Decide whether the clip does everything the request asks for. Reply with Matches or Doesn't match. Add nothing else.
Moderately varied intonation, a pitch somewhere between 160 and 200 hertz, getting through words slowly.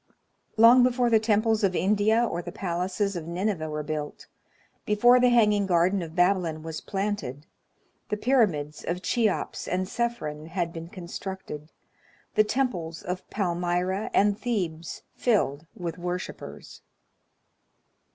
Matches